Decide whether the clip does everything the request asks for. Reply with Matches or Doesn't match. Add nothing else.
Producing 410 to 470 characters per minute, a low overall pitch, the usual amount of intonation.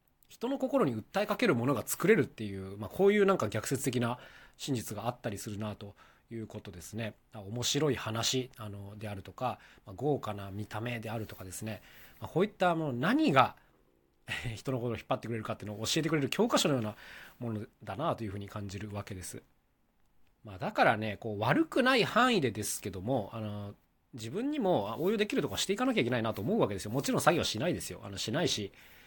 Matches